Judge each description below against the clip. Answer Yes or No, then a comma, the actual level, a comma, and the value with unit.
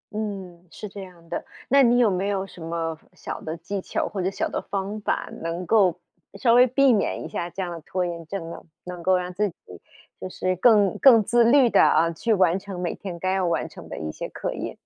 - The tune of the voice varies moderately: Yes, average, 3.4 semitones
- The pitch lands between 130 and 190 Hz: Yes, medium, 185 Hz